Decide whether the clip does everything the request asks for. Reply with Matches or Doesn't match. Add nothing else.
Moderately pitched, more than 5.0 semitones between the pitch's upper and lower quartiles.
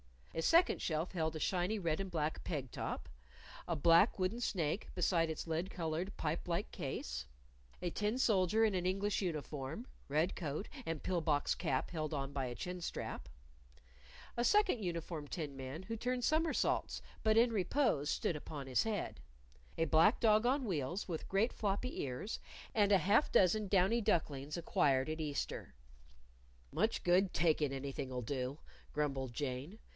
Matches